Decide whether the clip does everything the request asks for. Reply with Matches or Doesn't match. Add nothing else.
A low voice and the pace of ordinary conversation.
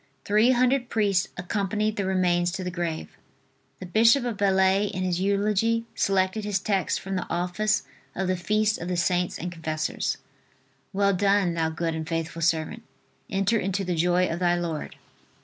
Doesn't match